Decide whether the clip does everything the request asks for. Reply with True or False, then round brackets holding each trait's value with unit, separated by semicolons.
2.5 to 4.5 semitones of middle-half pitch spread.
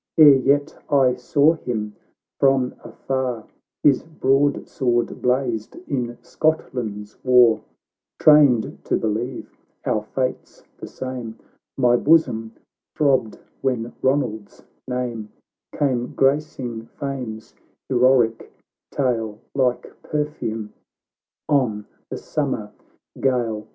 True (3.4 semitones)